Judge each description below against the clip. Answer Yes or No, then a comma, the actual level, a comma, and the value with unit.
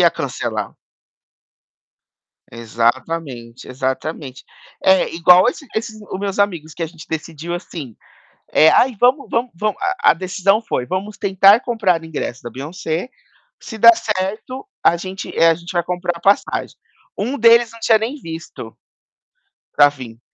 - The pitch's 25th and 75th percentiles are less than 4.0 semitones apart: No, wide, 5.4 semitones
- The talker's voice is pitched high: No, medium, 180 Hz